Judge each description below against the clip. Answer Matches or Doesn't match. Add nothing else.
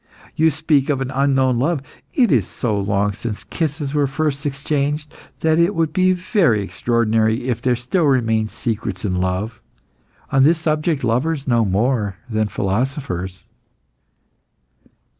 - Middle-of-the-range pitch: Doesn't match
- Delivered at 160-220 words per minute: Doesn't match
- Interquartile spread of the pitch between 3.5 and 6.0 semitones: Matches